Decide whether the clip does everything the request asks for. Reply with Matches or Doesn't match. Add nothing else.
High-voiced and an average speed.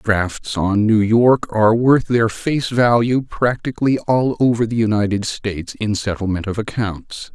Doesn't match